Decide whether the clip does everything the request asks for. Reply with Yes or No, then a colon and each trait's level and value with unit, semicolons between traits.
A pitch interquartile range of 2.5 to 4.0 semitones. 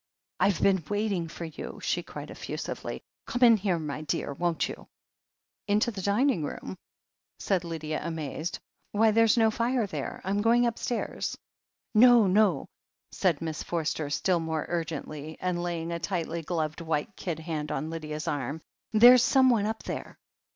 No: average, 5.3 semitones